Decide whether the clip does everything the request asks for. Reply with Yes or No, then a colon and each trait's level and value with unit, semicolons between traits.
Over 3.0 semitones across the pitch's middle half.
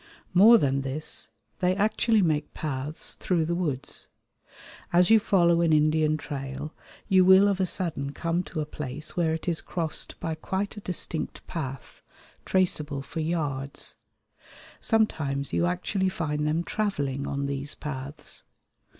Yes: average, 4.0 semitones